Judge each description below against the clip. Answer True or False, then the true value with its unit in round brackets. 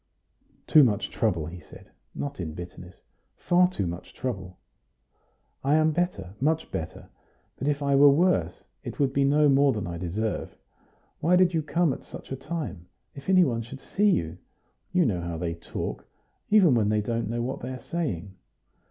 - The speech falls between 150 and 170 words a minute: False (185 wpm)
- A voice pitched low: True (130 Hz)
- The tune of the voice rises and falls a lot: True (9.0 semitones)